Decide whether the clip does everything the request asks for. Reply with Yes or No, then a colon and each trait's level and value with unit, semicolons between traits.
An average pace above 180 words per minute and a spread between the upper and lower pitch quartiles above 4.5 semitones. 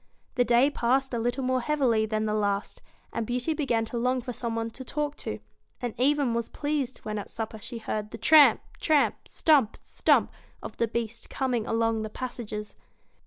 No: average, 190 wpm; average, 2.9 semitones